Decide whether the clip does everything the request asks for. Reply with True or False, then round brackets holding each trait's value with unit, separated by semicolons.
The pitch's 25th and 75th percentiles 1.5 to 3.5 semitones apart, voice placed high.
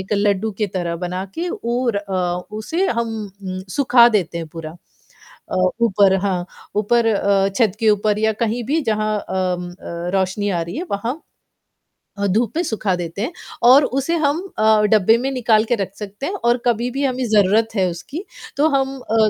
False (4.1 semitones; 215 Hz)